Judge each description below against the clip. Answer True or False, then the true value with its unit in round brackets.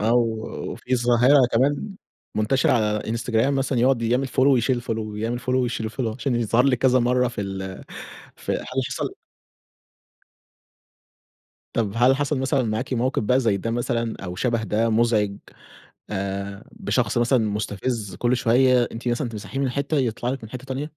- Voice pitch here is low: True (120 Hz)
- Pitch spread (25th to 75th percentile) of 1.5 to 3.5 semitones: True (2.8 semitones)